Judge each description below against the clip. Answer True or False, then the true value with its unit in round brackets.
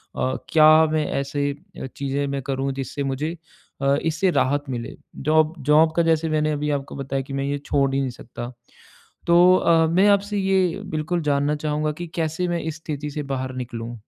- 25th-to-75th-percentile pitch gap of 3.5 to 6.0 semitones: False (2.9 semitones)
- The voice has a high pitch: False (150 Hz)